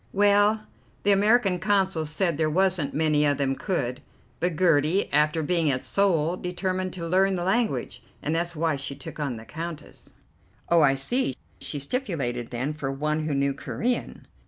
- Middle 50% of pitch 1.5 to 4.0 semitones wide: No, average, 4.7 semitones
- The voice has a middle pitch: Yes, medium, 165 Hz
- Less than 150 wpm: No, average, 170 wpm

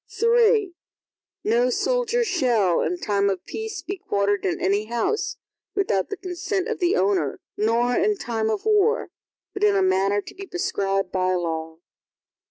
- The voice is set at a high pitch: Yes, high, 235 Hz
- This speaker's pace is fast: No, average, 160 wpm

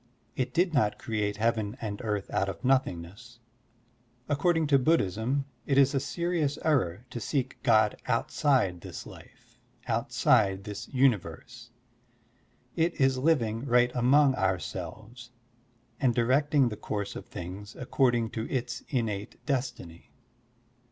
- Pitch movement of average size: Yes, average, 4.8 semitones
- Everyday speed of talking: No, slow, 130 wpm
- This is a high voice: No, low, 120 Hz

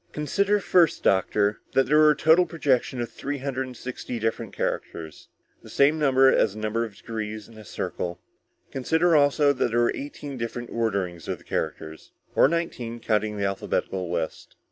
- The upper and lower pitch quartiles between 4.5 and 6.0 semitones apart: Yes, wide, 5.4 semitones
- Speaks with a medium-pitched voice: No, low, 120 Hz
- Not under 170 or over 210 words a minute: Yes, average, 180 wpm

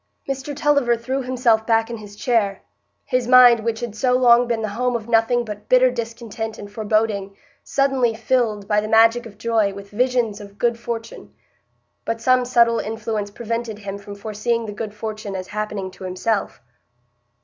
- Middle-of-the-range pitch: No, high, 225 Hz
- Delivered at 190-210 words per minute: No, average, 175 wpm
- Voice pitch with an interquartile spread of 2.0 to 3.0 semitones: Yes, narrow, 2.5 semitones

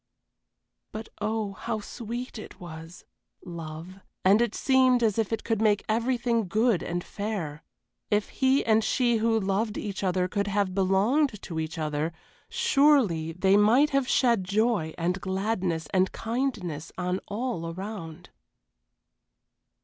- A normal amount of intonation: Yes, average, 4.3 semitones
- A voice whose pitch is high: Yes, high, 205 Hz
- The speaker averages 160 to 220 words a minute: No, average, 140 wpm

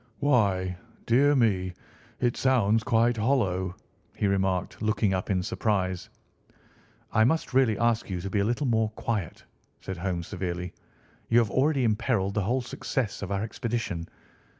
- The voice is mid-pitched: No, low, 105 Hz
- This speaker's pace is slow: No, average, 150 wpm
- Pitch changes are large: No, average, 4.1 semitones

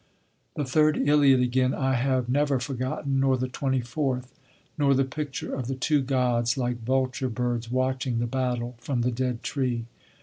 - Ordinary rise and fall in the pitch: No, narrow, 1.7 semitones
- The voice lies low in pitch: Yes, low, 130 Hz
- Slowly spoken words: No, average, 170 wpm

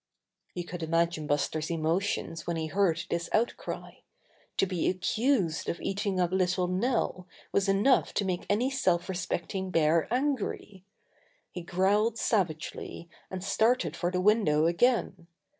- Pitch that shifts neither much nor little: Yes, average, 3.3 semitones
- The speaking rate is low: No, average, 145 wpm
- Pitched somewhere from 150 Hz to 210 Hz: Yes, medium, 185 Hz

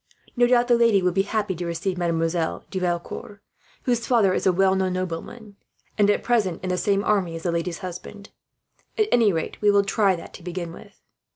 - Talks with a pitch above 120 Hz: Yes, high, 190 Hz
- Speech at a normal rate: No, fast, 210 wpm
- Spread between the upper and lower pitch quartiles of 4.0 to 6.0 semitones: No, average, 3.2 semitones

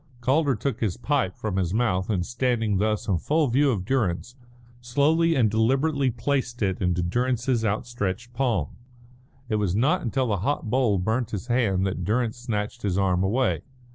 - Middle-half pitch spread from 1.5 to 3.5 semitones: No, average, 4.6 semitones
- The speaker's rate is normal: Yes, average, 170 wpm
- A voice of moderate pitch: No, low, 115 Hz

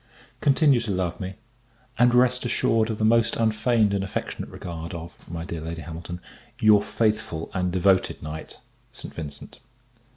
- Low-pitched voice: Yes, low, 100 Hz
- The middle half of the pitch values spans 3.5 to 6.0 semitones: Yes, average, 5.2 semitones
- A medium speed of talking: Yes, average, 155 wpm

